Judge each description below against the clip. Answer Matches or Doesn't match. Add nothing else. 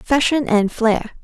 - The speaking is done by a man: Doesn't match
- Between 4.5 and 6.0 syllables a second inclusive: Matches